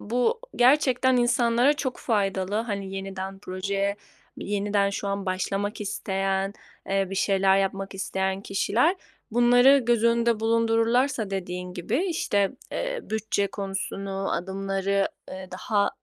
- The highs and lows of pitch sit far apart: No, average, 3.3 semitones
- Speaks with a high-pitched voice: Yes, high, 200 Hz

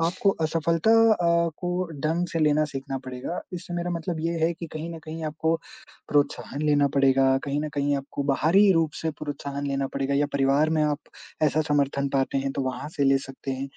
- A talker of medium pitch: Yes, medium, 150 Hz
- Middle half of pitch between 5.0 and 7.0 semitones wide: No, average, 3.0 semitones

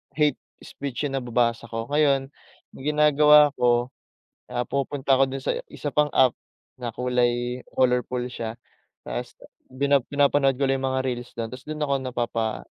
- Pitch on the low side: Yes, low, 130 Hz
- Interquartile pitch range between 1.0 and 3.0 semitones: Yes, average, 2.7 semitones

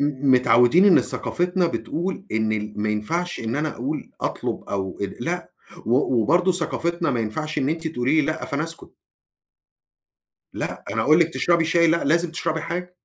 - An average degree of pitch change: No, wide, 5.7 semitones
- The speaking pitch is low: No, medium, 155 Hz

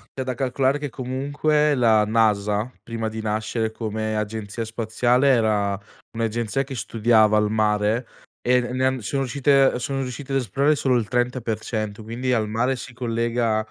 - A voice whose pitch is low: Yes, low, 115 Hz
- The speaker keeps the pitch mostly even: No, average, 3.1 semitones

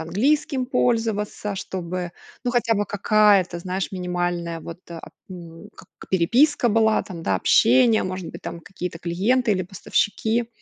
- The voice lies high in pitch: Yes, high, 195 Hz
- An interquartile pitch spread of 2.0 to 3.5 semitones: No, average, 4.4 semitones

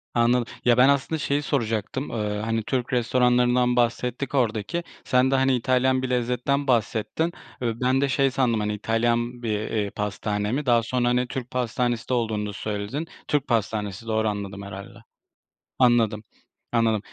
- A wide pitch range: No, average, 2.8 semitones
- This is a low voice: Yes, low, 120 Hz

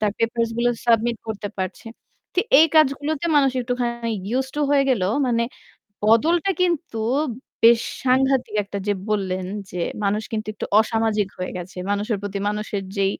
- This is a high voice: Yes, high, 230 Hz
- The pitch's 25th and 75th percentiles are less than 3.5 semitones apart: No, average, 4.1 semitones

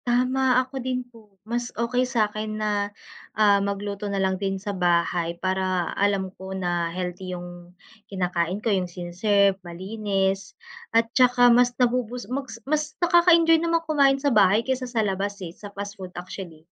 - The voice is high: Yes, high, 205 Hz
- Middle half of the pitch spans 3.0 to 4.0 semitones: No, average, 4.7 semitones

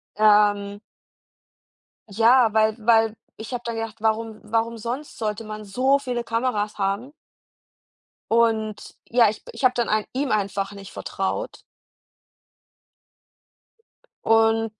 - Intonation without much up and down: Yes, narrow, 1.8 semitones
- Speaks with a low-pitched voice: No, high, 225 Hz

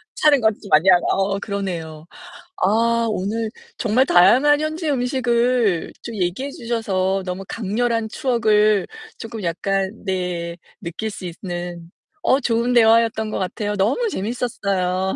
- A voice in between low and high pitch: No, high, 210 Hz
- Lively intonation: No, average, 4.1 semitones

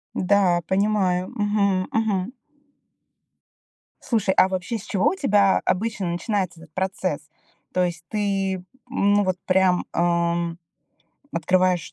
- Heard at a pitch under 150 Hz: No, high, 190 Hz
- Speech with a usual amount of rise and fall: No, narrow, 2.3 semitones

